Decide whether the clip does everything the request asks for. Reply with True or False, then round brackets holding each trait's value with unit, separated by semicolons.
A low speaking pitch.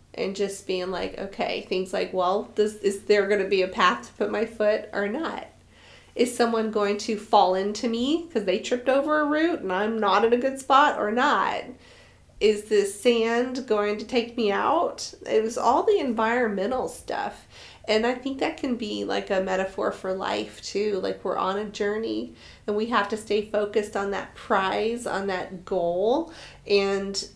False (210 Hz)